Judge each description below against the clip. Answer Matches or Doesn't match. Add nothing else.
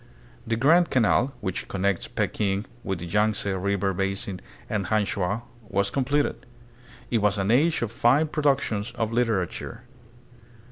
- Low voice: Matches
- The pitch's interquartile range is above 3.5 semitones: Matches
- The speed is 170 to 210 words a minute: Doesn't match